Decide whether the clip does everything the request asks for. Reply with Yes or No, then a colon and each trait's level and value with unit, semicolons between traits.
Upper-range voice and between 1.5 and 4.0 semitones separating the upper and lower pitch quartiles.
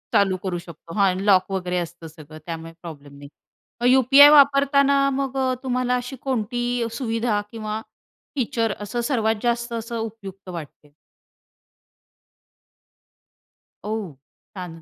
No: high, 220 Hz; wide, 5.5 semitones